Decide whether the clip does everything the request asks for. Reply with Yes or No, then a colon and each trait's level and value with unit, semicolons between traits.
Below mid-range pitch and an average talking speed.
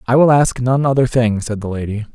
No: low, 120 Hz; fast, 250 wpm